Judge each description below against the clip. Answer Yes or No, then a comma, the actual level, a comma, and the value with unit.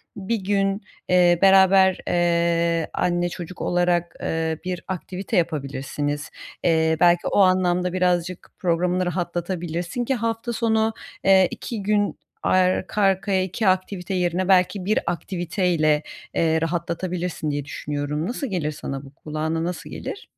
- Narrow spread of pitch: Yes, narrow, 2.3 semitones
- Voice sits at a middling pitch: Yes, medium, 180 Hz